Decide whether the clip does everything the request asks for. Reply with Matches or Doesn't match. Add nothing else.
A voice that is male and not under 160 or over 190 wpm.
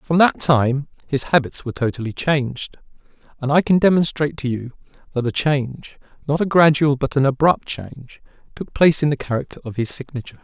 Matches